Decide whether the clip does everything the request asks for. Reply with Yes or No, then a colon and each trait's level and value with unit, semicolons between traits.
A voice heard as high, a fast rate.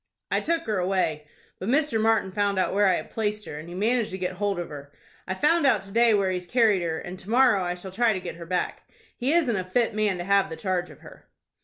Yes: high, 195 Hz; fast, 270 wpm